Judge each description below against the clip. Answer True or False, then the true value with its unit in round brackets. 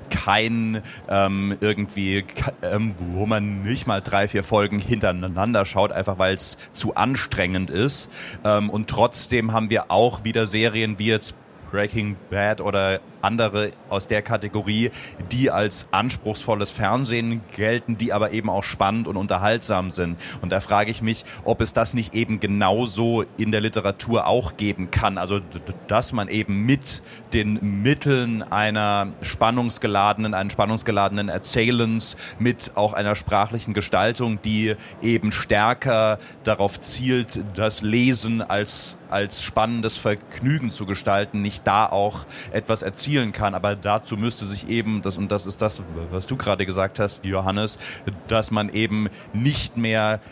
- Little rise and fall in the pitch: True (2.2 semitones)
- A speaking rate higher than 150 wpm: False (145 wpm)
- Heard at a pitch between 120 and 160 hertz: False (105 Hz)